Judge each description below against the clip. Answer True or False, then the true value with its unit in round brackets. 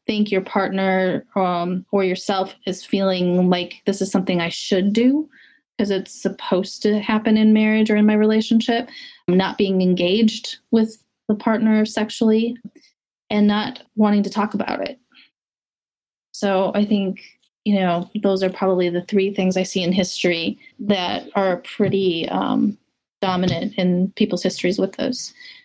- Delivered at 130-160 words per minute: True (155 wpm)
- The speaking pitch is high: True (200 Hz)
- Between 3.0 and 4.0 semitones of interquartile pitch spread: False (2.6 semitones)